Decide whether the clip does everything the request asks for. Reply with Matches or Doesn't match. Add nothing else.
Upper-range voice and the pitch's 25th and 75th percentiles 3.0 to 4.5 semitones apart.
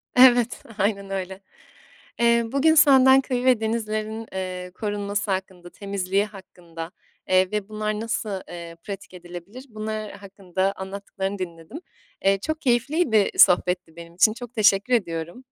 Matches